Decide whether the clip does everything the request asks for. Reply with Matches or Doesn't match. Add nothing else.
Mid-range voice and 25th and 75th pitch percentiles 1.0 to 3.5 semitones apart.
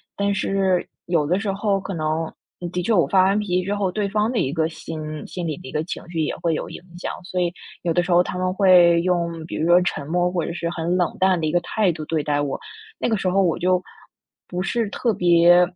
Matches